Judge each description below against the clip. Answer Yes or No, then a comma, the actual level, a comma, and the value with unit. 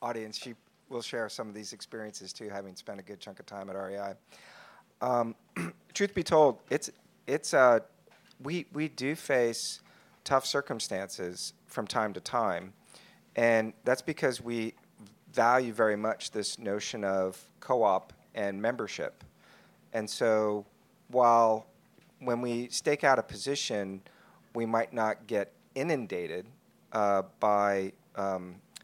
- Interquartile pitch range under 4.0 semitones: Yes, average, 3.5 semitones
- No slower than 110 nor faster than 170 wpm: Yes, slow, 135 wpm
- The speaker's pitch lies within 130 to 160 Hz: No, low, 110 Hz